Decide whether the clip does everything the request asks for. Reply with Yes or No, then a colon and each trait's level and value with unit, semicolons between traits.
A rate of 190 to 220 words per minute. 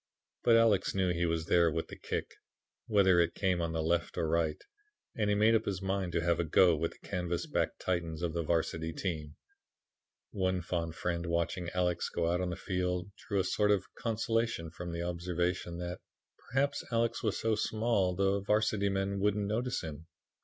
Yes: average, 195 wpm